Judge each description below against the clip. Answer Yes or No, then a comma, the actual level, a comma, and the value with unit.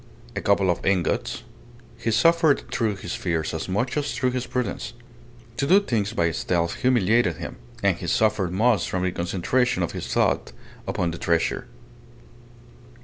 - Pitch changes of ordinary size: No, wide, 6.1 semitones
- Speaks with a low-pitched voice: Yes, low, 100 Hz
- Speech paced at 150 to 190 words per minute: Yes, average, 160 wpm